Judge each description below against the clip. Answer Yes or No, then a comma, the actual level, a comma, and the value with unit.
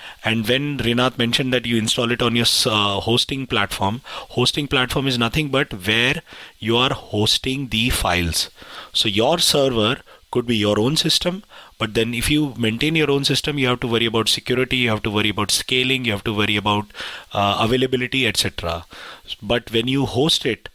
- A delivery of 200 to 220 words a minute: No, average, 190 wpm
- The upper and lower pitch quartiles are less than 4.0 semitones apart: Yes, average, 3.5 semitones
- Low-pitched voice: Yes, low, 120 Hz